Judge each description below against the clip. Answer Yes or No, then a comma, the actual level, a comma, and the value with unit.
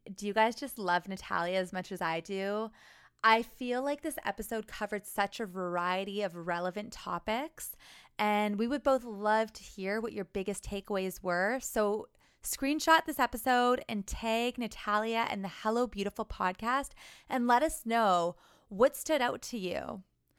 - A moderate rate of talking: Yes, average, 165 wpm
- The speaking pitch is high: Yes, high, 215 Hz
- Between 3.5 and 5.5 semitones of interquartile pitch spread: Yes, average, 3.8 semitones